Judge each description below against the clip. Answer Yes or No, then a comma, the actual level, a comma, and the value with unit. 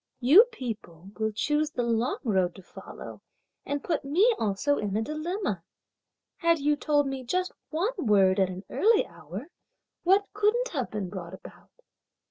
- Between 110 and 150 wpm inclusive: No, average, 160 wpm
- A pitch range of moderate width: No, wide, 9.0 semitones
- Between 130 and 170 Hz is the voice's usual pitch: No, very high, 270 Hz